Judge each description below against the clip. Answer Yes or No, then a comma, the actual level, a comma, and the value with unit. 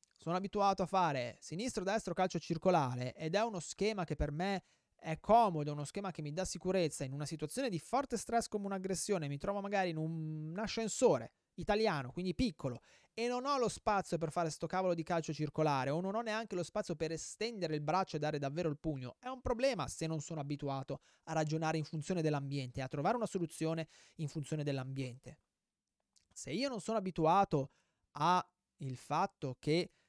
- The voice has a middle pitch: Yes, medium, 170 Hz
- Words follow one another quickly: Yes, fast, 185 wpm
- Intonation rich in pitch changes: No, average, 4.7 semitones